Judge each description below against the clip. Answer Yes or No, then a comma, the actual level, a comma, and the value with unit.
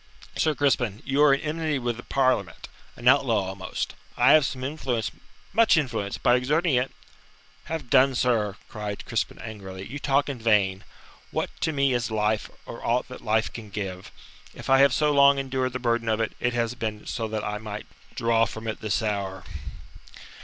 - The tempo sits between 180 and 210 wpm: Yes, average, 190 wpm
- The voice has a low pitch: Yes, low, 120 Hz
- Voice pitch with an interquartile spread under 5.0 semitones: Yes, average, 4.1 semitones